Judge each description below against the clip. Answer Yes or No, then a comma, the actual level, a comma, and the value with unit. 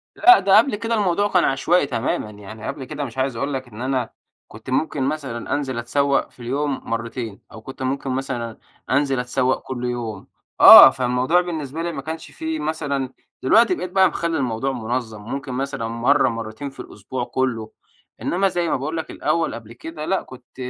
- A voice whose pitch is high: No, low, 135 Hz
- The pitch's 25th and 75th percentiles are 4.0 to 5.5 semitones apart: Yes, average, 4.7 semitones